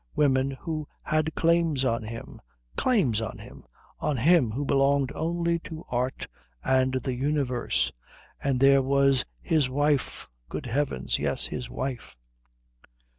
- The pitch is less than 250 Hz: Yes, low, 135 Hz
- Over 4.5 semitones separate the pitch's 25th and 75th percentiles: No, average, 3.1 semitones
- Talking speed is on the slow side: Yes, slow, 130 wpm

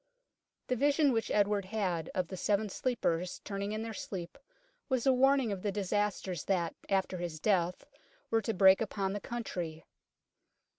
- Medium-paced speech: Yes, average, 160 wpm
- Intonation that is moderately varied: Yes, average, 3.5 semitones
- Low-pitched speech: No, high, 200 Hz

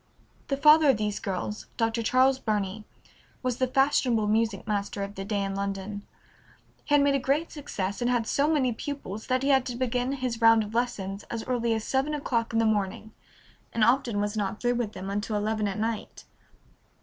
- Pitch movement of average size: Yes, average, 3.8 semitones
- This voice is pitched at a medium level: No, high, 225 Hz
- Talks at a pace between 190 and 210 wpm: Yes, average, 200 wpm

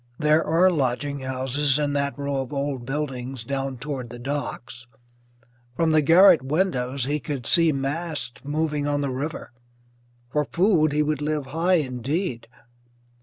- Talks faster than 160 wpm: No, average, 150 wpm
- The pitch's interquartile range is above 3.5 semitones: No, average, 2.7 semitones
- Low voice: No, medium, 145 Hz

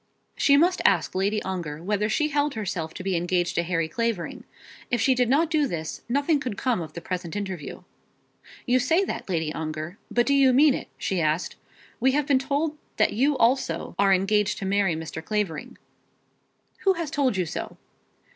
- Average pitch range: No, wide, 7.8 semitones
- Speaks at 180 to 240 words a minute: Yes, average, 190 wpm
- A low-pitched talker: No, high, 210 Hz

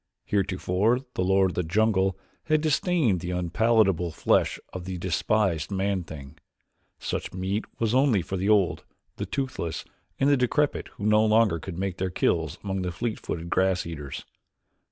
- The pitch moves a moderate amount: Yes, average, 3.7 semitones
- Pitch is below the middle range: Yes, very low, 95 Hz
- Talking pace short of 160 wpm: No, average, 165 wpm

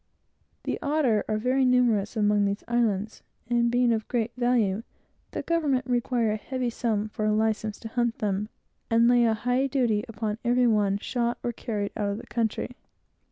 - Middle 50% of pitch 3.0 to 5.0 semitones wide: No, narrow, 2.5 semitones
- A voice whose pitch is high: Yes, high, 230 Hz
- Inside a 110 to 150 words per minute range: No, average, 180 wpm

